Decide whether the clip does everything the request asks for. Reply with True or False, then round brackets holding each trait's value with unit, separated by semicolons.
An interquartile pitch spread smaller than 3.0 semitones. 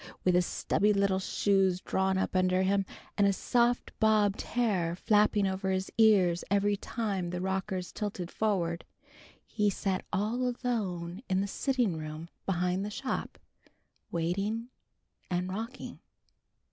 True (2.6 semitones)